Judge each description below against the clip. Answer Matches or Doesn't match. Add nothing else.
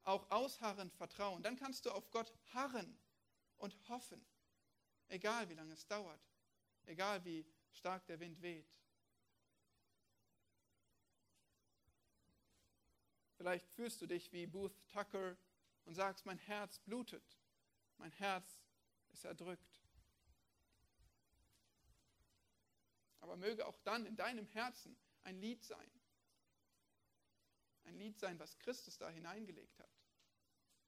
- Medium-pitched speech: Matches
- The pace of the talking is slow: Matches